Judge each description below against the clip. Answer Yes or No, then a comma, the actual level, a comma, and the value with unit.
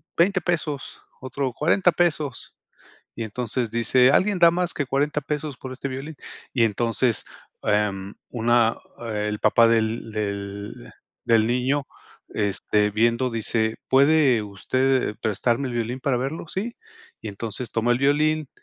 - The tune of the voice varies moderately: Yes, average, 4.5 semitones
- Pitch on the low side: Yes, low, 125 Hz